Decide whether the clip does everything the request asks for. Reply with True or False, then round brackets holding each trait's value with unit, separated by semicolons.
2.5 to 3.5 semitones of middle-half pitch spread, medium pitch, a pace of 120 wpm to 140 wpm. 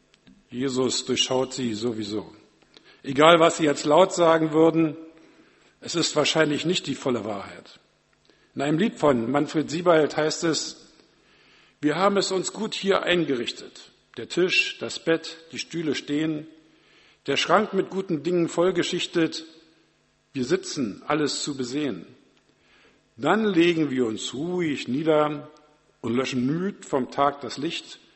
False (4.0 semitones; 155 Hz; 135 wpm)